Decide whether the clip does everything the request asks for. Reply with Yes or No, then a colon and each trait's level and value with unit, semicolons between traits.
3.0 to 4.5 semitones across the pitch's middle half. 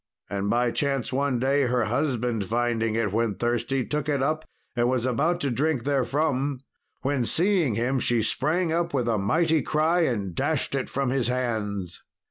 Yes: average, 3.8 semitones